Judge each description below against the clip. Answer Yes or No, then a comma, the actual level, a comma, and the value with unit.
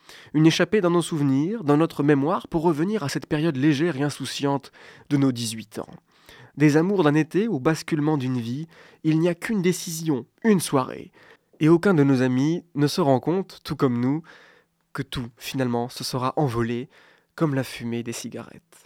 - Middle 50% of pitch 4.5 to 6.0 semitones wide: No, average, 3.9 semitones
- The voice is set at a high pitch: No, medium, 150 Hz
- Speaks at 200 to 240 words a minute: No, average, 185 wpm